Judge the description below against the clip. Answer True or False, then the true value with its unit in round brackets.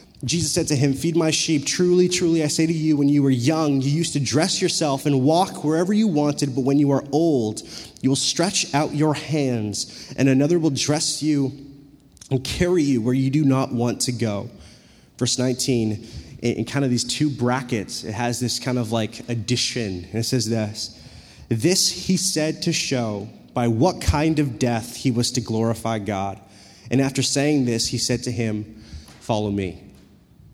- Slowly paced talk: False (190 wpm)